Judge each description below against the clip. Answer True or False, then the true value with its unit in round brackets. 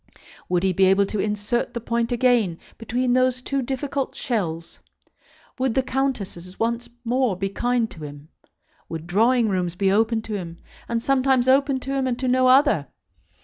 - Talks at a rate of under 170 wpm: False (175 wpm)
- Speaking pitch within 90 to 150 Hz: False (235 Hz)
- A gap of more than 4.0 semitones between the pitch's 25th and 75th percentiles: True (5.0 semitones)